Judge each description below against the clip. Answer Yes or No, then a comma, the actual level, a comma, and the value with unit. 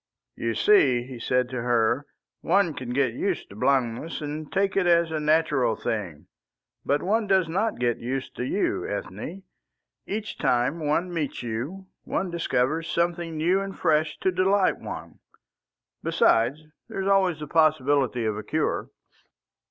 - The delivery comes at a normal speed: Yes, average, 155 wpm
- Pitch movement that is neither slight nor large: No, wide, 6.3 semitones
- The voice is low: No, medium, 155 Hz